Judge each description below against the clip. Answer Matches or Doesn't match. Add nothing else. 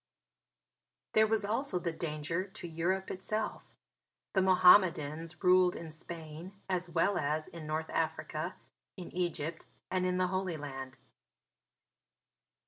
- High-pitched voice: Doesn't match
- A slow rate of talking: Matches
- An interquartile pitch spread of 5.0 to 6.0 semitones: Doesn't match